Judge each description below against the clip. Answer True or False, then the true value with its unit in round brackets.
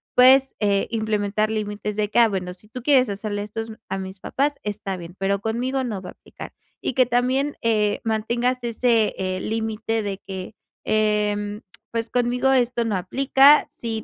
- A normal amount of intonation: True (3.0 semitones)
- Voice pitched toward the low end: False (220 Hz)